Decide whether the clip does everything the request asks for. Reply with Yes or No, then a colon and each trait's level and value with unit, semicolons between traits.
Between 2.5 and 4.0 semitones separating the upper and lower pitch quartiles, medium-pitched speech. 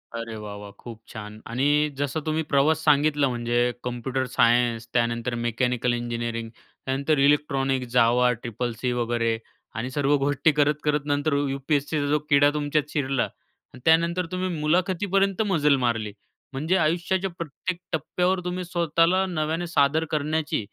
No: average, 4.8 semitones; medium, 145 Hz